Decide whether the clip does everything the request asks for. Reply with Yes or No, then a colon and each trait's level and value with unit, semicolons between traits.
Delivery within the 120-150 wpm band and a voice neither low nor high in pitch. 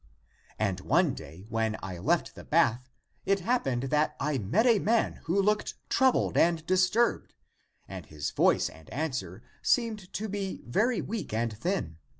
No: average, 165 wpm; medium, 160 Hz